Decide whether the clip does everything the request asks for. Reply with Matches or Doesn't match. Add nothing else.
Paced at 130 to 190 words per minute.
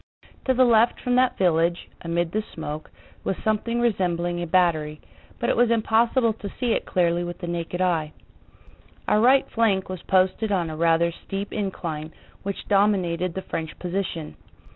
Matches